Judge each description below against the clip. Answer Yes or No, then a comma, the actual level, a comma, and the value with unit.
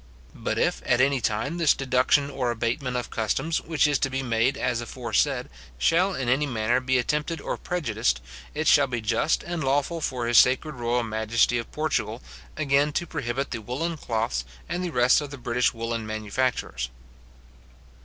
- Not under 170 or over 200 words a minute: Yes, average, 175 wpm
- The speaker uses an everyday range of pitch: Yes, average, 3.8 semitones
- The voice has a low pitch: Yes, low, 130 Hz